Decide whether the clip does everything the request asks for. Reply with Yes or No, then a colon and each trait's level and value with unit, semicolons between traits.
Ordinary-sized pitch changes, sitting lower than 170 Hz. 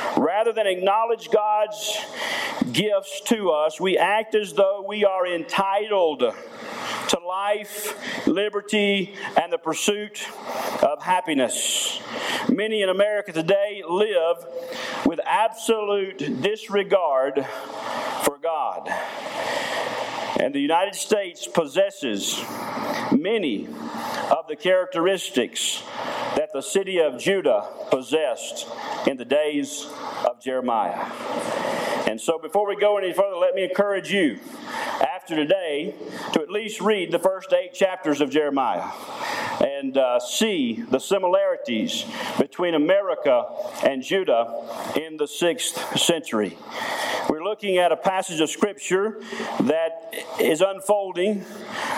No: average, 4.1 semitones; high, 205 Hz